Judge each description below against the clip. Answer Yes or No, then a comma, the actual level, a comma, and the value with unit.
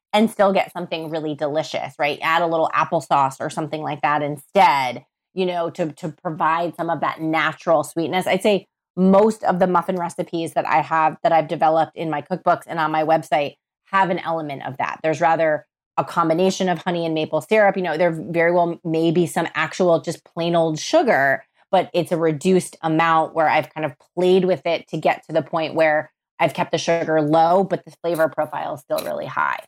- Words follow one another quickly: Yes, fast, 210 wpm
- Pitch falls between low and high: Yes, medium, 165 Hz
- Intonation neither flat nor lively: No, narrow, 2.1 semitones